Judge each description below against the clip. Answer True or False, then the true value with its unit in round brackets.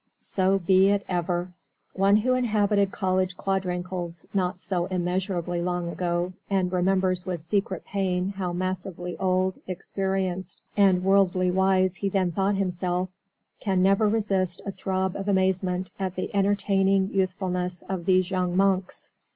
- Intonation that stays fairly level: True (1.3 semitones)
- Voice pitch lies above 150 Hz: True (185 Hz)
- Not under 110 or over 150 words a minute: True (140 wpm)